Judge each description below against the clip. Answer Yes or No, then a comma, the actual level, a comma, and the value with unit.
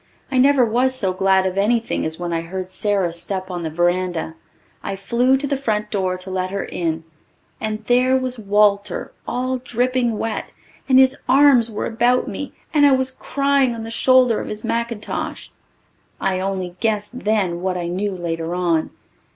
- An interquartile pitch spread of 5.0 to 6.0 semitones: Yes, wide, 5.4 semitones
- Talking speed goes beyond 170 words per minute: Yes, average, 180 wpm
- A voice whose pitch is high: Yes, high, 210 Hz